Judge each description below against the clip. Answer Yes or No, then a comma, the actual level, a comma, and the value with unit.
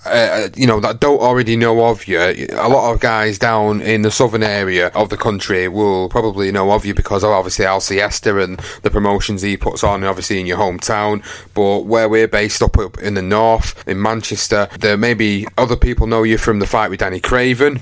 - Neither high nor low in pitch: No, low, 105 Hz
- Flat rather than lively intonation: Yes, narrow, 2.2 semitones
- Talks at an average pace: No, fast, 220 wpm